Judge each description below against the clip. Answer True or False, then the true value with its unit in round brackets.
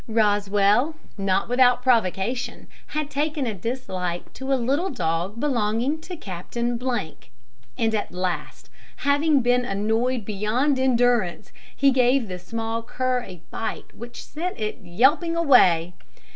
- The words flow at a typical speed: False (130 wpm)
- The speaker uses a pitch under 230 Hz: False (235 Hz)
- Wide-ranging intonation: False (4.6 semitones)